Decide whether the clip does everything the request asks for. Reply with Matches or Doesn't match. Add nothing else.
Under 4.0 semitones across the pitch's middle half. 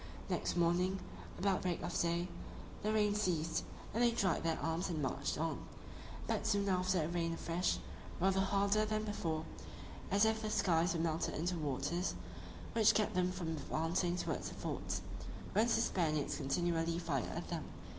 Matches